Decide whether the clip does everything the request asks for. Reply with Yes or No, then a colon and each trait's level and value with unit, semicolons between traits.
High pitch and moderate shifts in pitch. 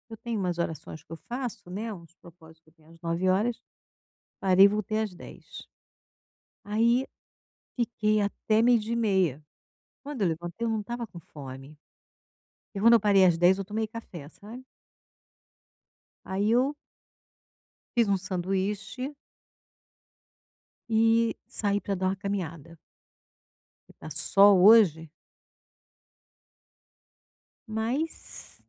Yes: high, 200 Hz; average, 4.5 semitones